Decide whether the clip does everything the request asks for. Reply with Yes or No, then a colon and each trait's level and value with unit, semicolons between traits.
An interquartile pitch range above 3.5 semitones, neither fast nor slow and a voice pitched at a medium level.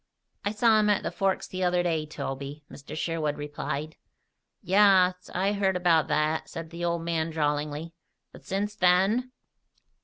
Yes: average, 3.9 semitones; average, 155 wpm; medium, 170 Hz